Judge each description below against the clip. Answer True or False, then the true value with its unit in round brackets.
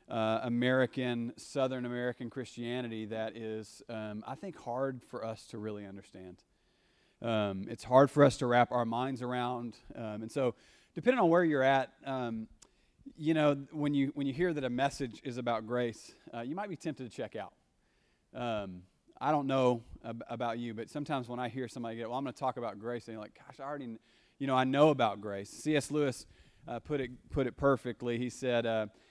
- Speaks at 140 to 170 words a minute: False (205 wpm)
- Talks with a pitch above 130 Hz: False (120 Hz)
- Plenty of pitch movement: False (3.2 semitones)